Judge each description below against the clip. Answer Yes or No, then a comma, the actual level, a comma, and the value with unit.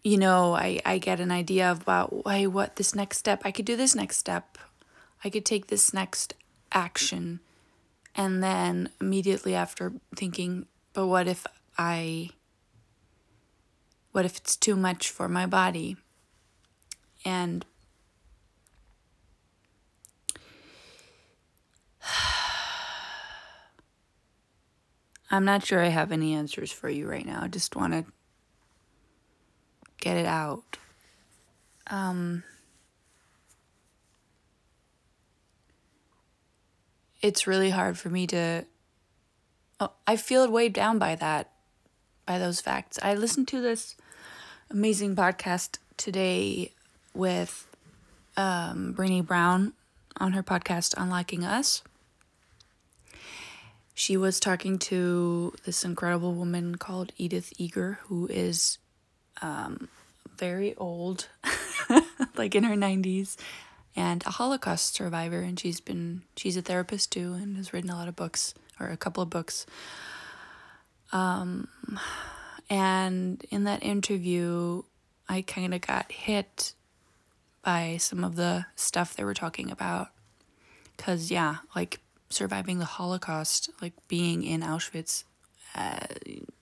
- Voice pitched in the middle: Yes, medium, 180 Hz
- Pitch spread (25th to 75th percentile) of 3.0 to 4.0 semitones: Yes, average, 3.4 semitones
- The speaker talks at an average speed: No, slow, 115 wpm